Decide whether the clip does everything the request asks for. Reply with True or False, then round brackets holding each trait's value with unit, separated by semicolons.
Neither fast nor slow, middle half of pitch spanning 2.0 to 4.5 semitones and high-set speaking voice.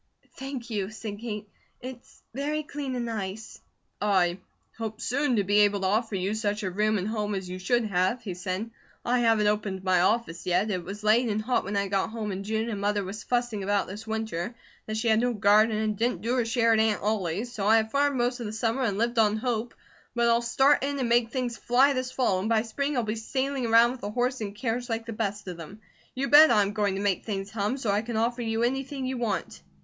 False (245 wpm; 3.0 semitones; 220 Hz)